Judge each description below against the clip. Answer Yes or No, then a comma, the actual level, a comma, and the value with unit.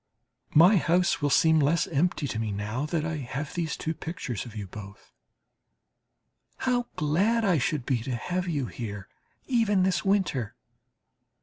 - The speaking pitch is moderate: Yes, medium, 155 Hz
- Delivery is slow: No, average, 150 wpm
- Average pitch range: No, wide, 6.6 semitones